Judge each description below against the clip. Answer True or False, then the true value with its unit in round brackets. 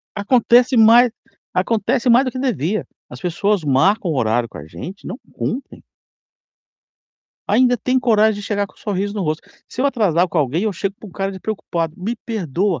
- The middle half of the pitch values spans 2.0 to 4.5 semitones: False (5.0 semitones)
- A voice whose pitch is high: True (205 Hz)